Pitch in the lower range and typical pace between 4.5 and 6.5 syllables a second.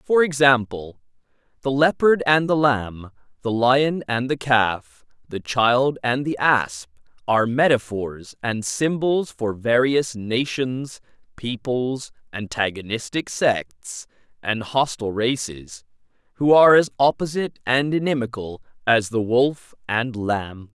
No: low, 125 Hz; 3.8 syllables/s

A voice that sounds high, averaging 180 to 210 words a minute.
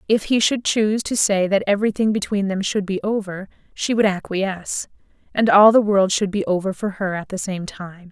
Yes: high, 200 Hz; fast, 205 wpm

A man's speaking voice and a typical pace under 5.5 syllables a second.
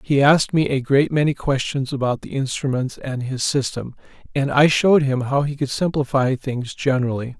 Yes: male; 5.2 syllables/s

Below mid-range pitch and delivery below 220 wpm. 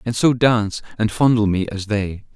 Yes: low, 110 Hz; fast, 205 wpm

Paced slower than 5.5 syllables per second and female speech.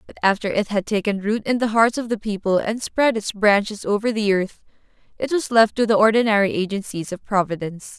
No: 5.7 syllables/s; female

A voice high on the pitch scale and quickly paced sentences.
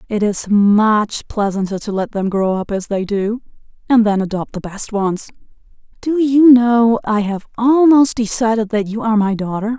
No: high, 215 Hz; average, 185 wpm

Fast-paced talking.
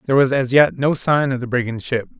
Yes: fast, 275 wpm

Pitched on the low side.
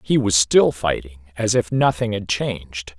Yes: low, 100 Hz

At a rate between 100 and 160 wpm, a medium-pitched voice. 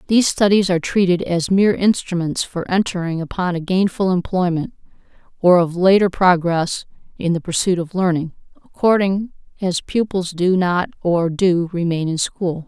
Yes: average, 150 wpm; medium, 180 Hz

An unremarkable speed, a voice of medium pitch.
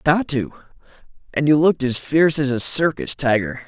Yes: average, 195 wpm; medium, 145 Hz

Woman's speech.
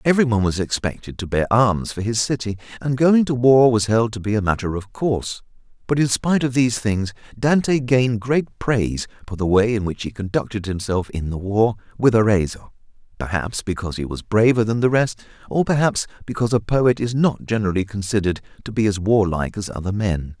No: male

